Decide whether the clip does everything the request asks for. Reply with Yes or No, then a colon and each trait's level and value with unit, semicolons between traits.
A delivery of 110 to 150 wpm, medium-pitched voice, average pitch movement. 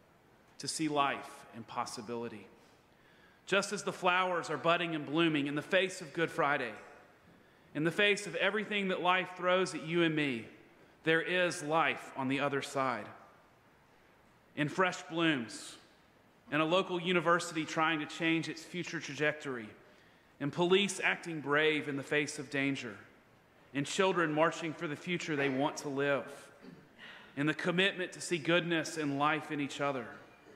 No: average, 160 wpm; medium, 155 Hz; average, 3.7 semitones